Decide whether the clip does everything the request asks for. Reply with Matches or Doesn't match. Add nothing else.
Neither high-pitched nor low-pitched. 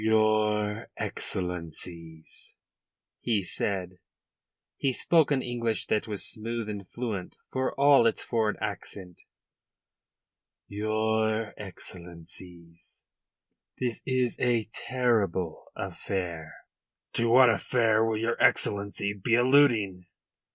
Doesn't match